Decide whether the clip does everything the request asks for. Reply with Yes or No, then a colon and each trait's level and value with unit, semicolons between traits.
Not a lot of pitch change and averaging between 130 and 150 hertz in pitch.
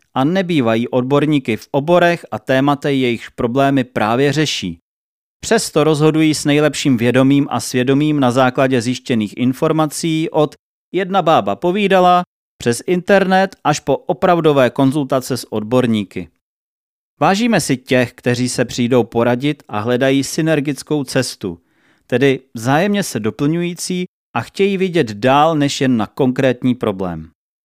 No: average, 4.2 semitones; low, 135 Hz